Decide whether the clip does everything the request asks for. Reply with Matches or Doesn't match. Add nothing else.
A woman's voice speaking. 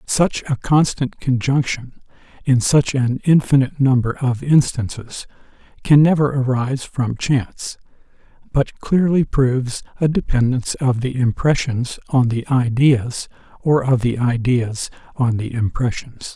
Doesn't match